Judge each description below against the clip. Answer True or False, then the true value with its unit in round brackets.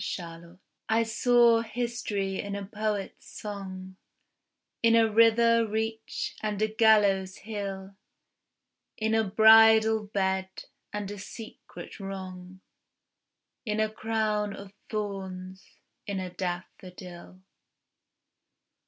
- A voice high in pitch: True (205 Hz)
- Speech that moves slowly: True (100 wpm)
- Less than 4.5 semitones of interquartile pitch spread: True (2.6 semitones)